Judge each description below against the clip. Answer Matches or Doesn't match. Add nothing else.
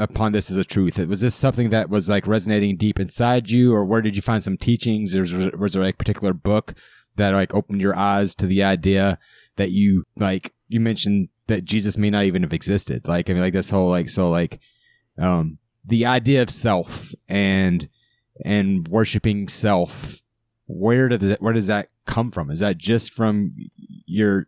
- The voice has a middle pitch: Doesn't match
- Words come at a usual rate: Matches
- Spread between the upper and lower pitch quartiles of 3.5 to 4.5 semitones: Doesn't match